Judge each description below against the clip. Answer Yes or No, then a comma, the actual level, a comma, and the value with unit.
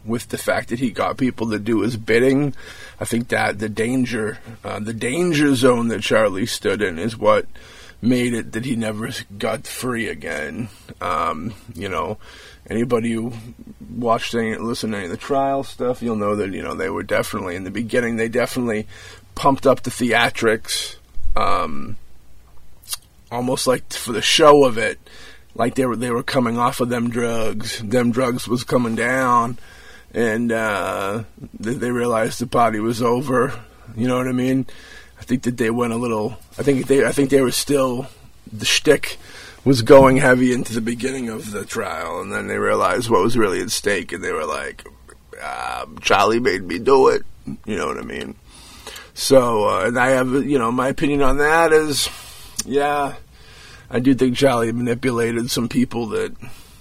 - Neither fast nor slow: Yes, average, 180 wpm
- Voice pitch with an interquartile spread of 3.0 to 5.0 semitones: No, narrow, 2.4 semitones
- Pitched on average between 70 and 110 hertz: No, low, 120 Hz